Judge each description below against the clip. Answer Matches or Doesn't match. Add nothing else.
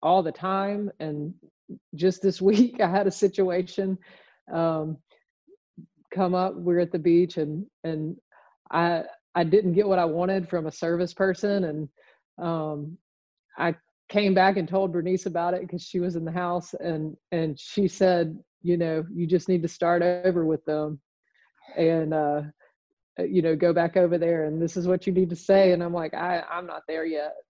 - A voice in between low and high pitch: Matches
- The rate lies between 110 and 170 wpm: Doesn't match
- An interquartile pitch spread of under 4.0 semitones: Matches